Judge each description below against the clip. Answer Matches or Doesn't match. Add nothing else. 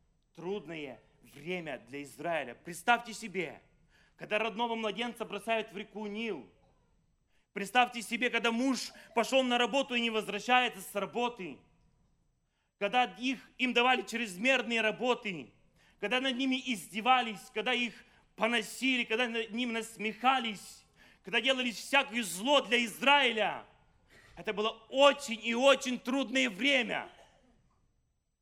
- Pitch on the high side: Matches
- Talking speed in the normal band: Doesn't match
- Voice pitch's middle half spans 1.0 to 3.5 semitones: Matches